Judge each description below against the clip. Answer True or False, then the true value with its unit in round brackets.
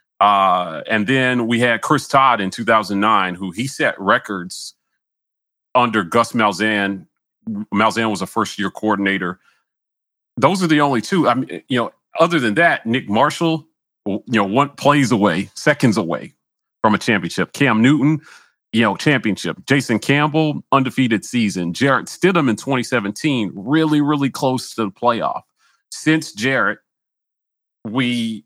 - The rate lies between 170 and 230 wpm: False (145 wpm)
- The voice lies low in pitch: True (120 Hz)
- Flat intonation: False (4.7 semitones)